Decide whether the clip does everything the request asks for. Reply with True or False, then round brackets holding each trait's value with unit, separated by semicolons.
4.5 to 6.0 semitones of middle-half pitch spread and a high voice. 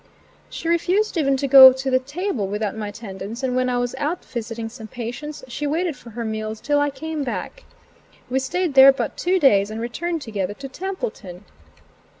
True (5.2 semitones; 260 Hz)